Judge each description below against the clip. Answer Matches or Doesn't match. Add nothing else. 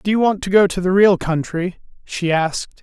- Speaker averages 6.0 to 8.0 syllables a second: Doesn't match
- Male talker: Matches